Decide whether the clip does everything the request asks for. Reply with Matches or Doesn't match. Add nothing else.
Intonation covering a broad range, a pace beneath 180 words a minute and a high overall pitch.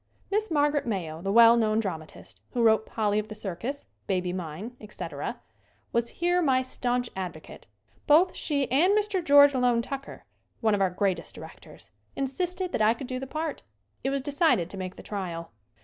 Doesn't match